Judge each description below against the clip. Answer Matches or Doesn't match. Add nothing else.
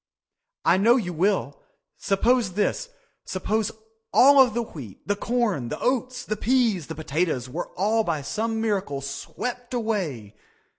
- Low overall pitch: Doesn't match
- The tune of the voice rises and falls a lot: Matches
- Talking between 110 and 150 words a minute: Matches